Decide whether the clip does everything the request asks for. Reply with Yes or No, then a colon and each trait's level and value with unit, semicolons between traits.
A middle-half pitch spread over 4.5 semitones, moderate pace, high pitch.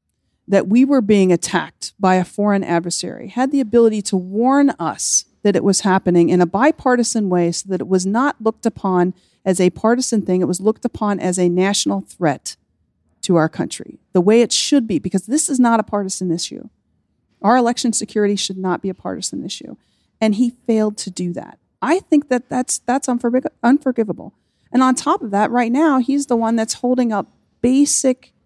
Yes: average, 5.2 semitones; average, 195 wpm; high, 215 Hz